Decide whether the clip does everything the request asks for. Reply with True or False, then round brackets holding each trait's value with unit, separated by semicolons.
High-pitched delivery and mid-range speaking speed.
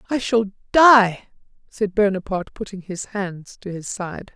True (200 Hz; 150 wpm)